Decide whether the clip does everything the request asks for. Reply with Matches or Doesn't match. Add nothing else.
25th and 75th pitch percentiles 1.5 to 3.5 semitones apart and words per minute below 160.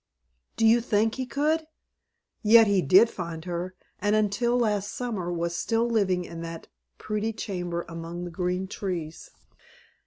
Doesn't match